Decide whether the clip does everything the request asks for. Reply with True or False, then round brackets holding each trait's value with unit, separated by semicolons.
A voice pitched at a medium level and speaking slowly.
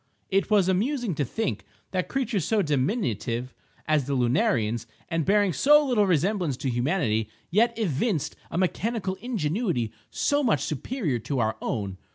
False (175 Hz; 150 wpm)